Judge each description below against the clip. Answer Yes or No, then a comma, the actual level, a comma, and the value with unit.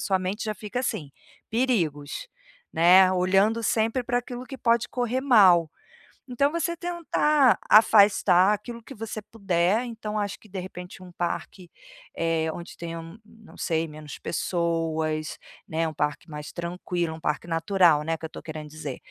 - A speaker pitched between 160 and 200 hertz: Yes, medium, 185 Hz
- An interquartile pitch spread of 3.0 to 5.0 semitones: No, wide, 5.5 semitones